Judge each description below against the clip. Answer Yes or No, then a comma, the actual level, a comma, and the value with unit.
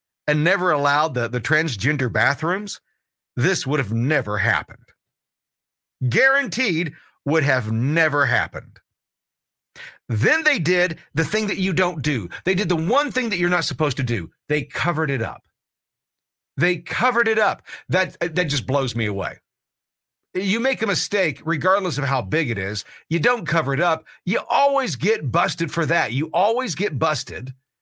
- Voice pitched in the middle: Yes, medium, 160 Hz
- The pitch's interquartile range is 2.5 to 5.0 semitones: No, wide, 5.6 semitones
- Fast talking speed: No, average, 165 wpm